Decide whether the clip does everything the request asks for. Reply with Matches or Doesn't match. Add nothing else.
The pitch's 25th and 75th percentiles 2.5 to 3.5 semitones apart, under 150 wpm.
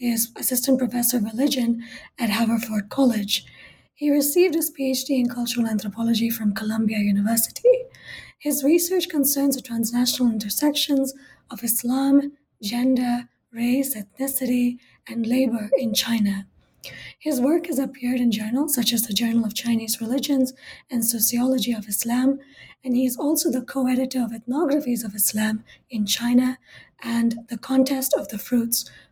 Matches